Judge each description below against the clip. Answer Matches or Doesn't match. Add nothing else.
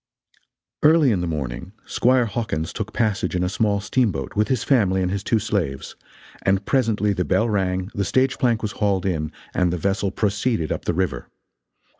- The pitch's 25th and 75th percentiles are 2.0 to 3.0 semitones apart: Doesn't match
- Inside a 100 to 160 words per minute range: Doesn't match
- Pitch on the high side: Doesn't match